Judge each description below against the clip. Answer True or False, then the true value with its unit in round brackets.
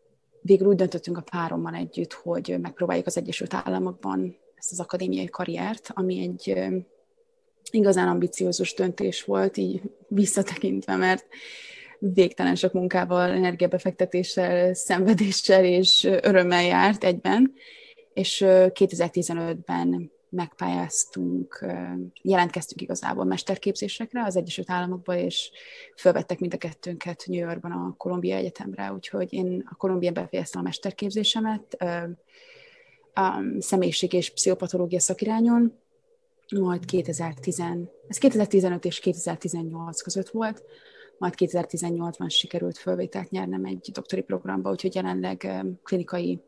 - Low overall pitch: False (180 Hz)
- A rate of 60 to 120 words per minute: True (105 wpm)